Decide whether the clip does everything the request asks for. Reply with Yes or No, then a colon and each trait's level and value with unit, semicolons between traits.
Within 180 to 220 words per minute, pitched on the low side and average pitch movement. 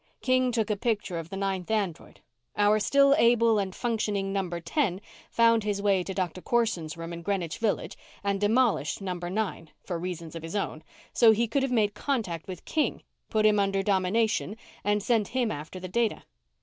No: average, 190 wpm; high, 205 Hz; average, 3.7 semitones